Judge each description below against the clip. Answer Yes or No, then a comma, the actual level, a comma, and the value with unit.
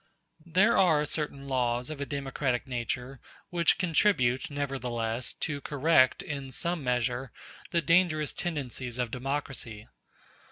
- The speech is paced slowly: Yes, slow, 120 wpm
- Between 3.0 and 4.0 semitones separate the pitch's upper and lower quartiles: Yes, average, 3.7 semitones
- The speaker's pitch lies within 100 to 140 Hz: Yes, low, 135 Hz